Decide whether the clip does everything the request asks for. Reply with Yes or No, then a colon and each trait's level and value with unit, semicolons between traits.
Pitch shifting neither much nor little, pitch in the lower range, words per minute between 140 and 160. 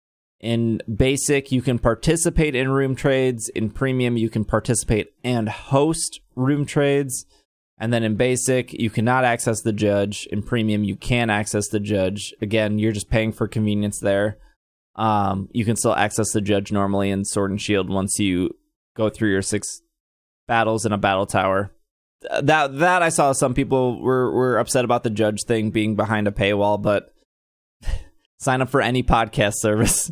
No: average, 3.7 semitones; low, 110 Hz; average, 175 wpm